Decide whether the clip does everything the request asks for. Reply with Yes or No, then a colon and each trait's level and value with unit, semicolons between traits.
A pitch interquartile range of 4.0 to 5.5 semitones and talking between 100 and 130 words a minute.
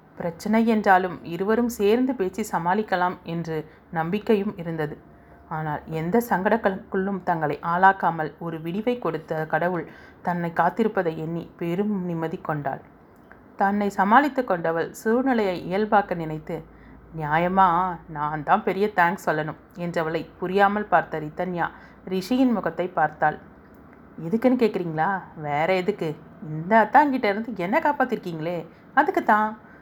Yes: average, 4.3 semitones; average, 105 wpm